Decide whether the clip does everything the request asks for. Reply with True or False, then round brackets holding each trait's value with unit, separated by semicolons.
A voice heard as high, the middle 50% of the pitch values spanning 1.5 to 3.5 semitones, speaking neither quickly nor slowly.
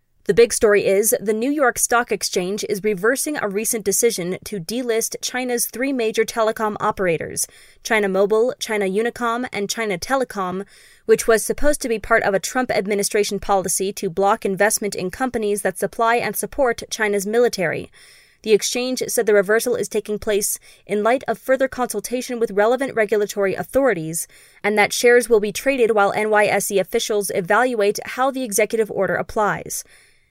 True (220 Hz; 2.8 semitones; 160 wpm)